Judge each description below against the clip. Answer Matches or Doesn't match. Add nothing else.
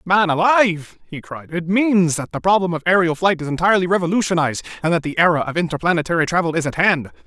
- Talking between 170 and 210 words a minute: Matches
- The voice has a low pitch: Doesn't match